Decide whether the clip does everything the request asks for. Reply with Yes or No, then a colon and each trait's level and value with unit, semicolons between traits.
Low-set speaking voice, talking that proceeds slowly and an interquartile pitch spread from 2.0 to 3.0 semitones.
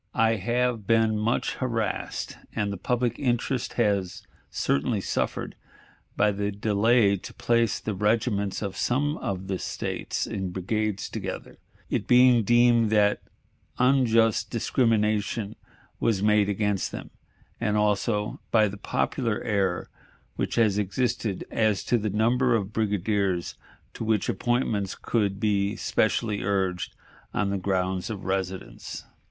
Yes: low, 105 Hz; slow, 130 wpm; average, 2.7 semitones